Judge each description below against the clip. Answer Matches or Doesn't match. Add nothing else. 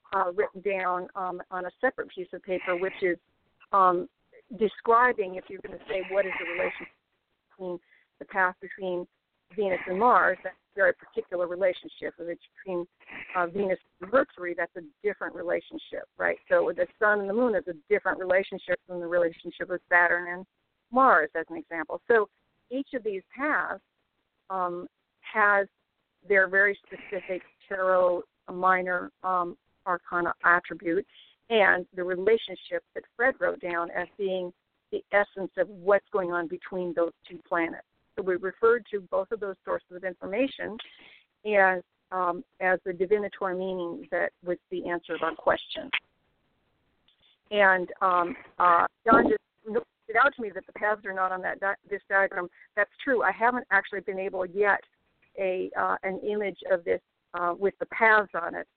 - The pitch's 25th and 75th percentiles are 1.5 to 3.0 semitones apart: Matches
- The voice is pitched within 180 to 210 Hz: Matches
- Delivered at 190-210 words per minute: Doesn't match